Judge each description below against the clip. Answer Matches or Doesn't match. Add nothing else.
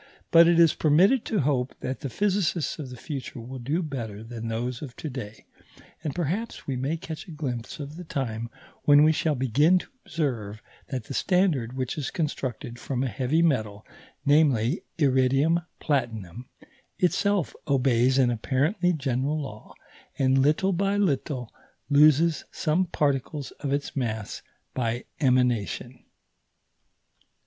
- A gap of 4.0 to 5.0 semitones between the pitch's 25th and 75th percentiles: Matches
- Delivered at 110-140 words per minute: Doesn't match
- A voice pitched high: Doesn't match